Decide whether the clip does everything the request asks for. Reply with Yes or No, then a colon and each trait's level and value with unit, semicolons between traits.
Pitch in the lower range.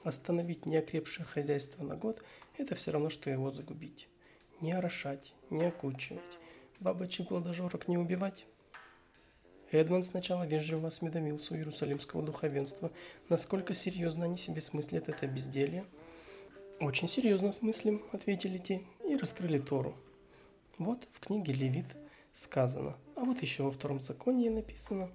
No: medium, 165 Hz